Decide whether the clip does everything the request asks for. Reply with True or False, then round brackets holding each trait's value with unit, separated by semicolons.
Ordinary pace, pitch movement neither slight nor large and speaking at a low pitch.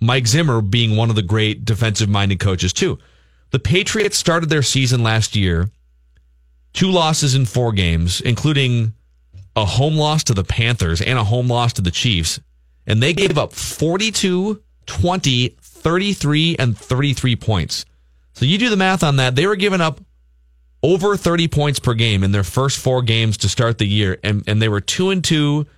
False (185 wpm; 7.3 semitones; 120 Hz)